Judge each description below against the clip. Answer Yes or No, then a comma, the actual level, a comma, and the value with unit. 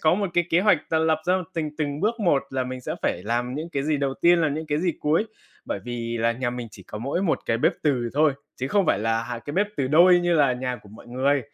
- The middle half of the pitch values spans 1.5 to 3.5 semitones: No, average, 5.1 semitones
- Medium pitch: Yes, medium, 145 Hz